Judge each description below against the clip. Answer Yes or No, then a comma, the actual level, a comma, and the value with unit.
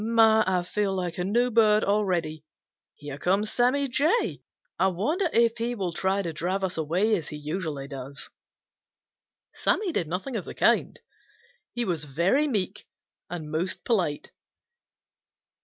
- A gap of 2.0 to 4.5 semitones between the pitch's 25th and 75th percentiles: No, wide, 5.6 semitones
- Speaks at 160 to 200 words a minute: No, average, 150 wpm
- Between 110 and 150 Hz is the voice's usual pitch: No, high, 190 Hz